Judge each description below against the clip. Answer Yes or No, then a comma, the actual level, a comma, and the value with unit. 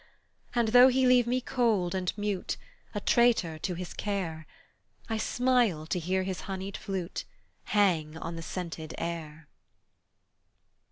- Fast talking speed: No, slow, 135 wpm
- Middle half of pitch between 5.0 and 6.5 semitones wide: Yes, average, 5.3 semitones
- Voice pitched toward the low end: No, high, 190 Hz